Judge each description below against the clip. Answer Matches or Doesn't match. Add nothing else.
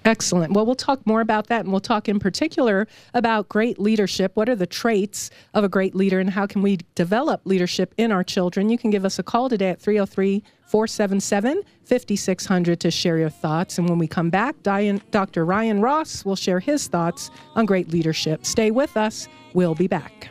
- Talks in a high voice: Matches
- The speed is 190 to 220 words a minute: Matches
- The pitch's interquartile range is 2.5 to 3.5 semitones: Matches